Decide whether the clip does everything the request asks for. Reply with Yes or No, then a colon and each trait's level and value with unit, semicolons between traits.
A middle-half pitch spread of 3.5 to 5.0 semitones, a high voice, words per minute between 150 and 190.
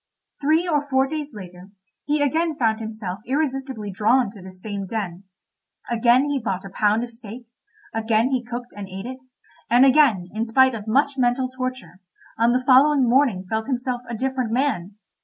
Yes: average, 3.8 semitones; high, 240 Hz; average, 175 wpm